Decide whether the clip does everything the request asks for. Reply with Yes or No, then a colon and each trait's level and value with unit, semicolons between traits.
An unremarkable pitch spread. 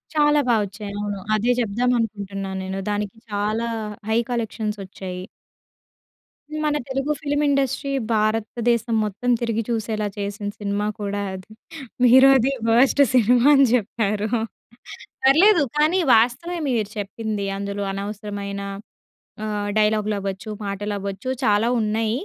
Yes: average, 3.2 semitones